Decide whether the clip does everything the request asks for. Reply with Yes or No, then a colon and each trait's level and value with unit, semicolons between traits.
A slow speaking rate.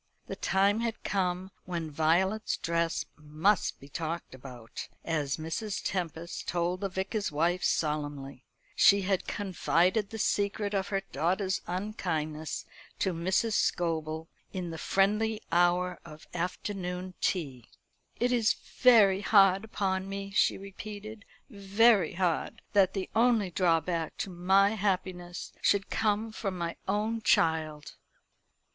Yes: slow, 125 wpm